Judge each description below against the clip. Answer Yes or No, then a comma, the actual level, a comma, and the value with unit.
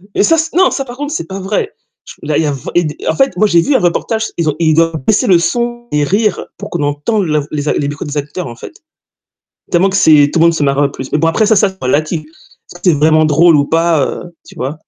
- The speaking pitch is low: No, medium, 165 Hz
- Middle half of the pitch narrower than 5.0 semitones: No, average, 5.3 semitones